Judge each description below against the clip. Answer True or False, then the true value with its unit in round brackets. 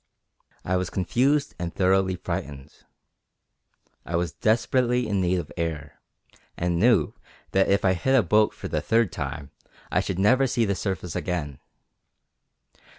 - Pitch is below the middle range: True (95 Hz)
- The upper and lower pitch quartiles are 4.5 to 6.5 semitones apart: True (5.0 semitones)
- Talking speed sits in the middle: True (150 wpm)